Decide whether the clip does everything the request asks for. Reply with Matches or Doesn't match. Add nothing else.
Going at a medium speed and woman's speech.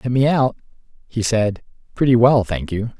Doesn't match